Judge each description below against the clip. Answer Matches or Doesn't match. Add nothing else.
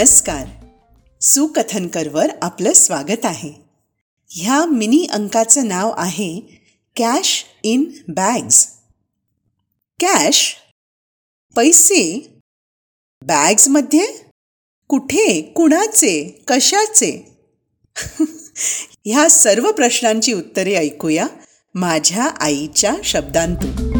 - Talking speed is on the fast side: Doesn't match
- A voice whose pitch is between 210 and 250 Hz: Matches